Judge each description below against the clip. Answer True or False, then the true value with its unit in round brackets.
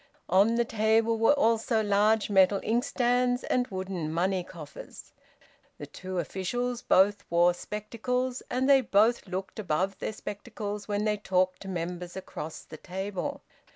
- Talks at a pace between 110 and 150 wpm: True (145 wpm)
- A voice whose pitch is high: True (205 Hz)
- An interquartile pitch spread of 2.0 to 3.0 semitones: False (3.8 semitones)